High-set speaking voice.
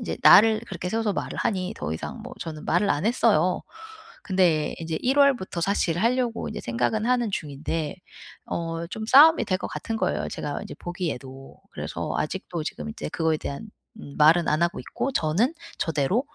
No: medium, 180 Hz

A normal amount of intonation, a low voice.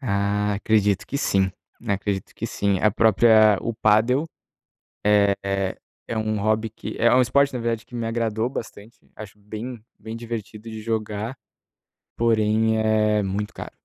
No: narrow, 1.8 semitones; low, 110 Hz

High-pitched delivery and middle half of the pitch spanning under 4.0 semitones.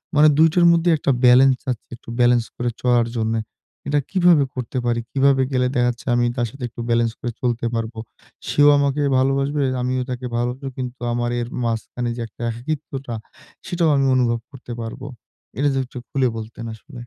No: low, 125 Hz; narrow, 2.6 semitones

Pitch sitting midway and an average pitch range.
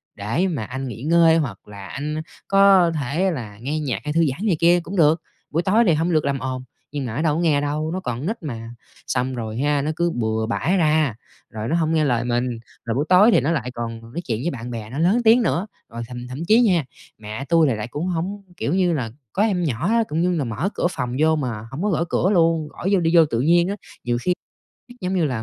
No: medium, 150 Hz; wide, 5.9 semitones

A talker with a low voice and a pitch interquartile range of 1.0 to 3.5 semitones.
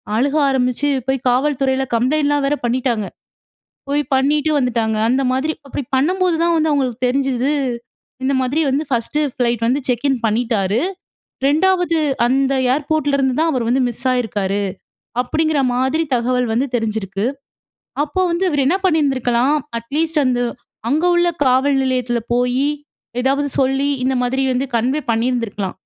No: very high, 265 Hz; average, 3.1 semitones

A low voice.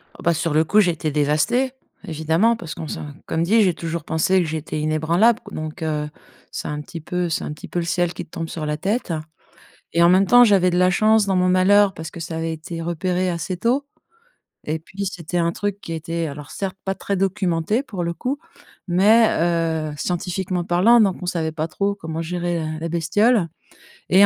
No: medium, 175 Hz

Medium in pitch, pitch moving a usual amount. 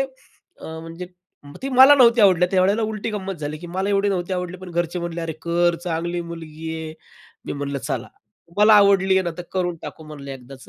Yes: medium, 175 Hz; average, 3.5 semitones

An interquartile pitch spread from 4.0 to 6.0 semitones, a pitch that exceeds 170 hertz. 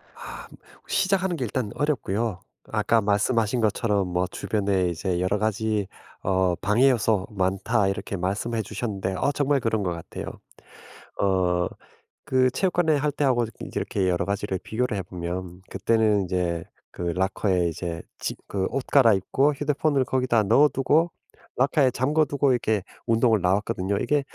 No: wide, 5.4 semitones; low, 105 Hz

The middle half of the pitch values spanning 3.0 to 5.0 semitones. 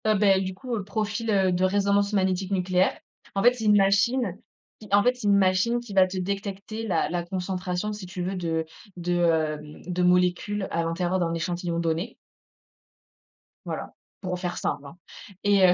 No: narrow, 2.4 semitones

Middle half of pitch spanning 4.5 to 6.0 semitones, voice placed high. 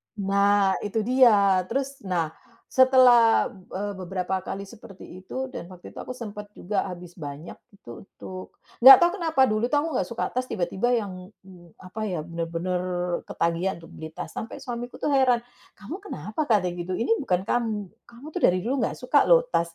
Yes: average, 5.2 semitones; high, 205 Hz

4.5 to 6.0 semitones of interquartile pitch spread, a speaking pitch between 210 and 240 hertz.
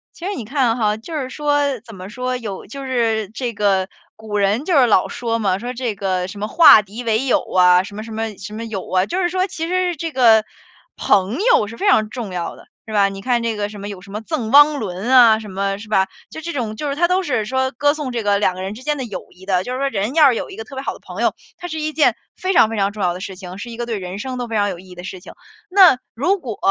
Yes: average, 5.2 semitones; high, 225 Hz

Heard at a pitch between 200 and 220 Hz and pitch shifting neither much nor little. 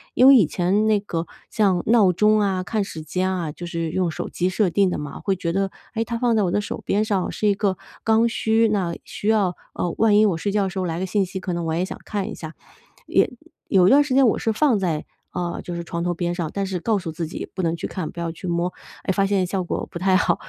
No: high, 190 Hz; average, 3.3 semitones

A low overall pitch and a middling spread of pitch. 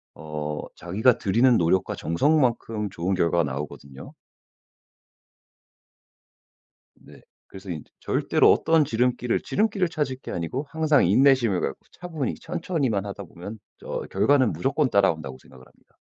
No: low, 110 Hz; wide, 8.5 semitones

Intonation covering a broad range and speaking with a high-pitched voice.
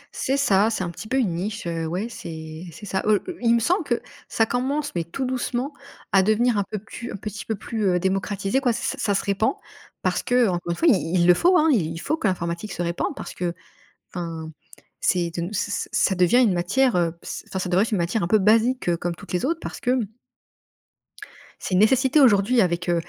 Yes: wide, 5.7 semitones; high, 200 Hz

